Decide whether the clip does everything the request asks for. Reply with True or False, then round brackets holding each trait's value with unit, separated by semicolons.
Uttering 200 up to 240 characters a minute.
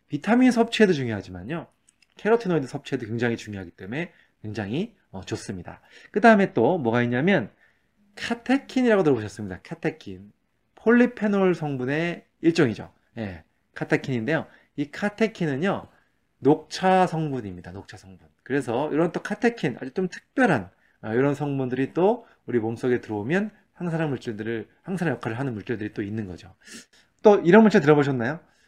False (350 characters per minute)